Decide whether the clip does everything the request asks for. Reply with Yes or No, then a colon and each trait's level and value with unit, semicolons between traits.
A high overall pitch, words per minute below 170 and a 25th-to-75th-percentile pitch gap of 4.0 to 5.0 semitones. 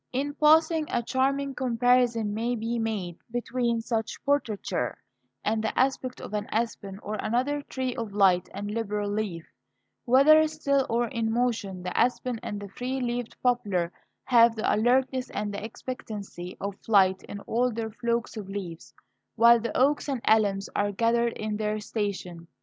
No: high, 230 Hz; average, 160 wpm; average, 3.4 semitones